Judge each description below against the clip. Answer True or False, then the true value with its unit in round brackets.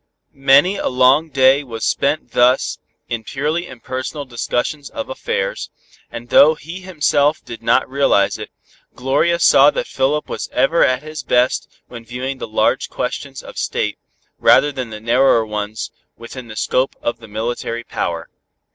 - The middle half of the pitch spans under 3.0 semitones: False (4.1 semitones)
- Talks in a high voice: False (130 Hz)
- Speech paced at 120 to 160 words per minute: True (155 wpm)